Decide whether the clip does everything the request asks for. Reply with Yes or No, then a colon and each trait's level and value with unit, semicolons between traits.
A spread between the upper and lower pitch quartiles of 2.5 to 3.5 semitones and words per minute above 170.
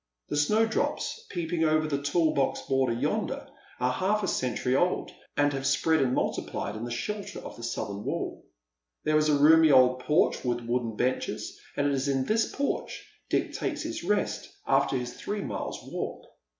No: average, 4.3 semitones; average, 180 wpm